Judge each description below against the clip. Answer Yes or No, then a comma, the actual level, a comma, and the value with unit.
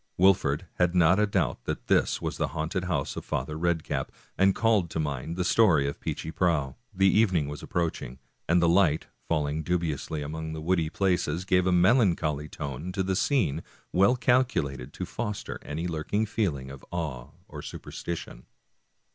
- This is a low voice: Yes, very low, 85 Hz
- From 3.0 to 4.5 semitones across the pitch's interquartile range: Yes, average, 3.9 semitones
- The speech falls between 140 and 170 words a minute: No, average, 180 wpm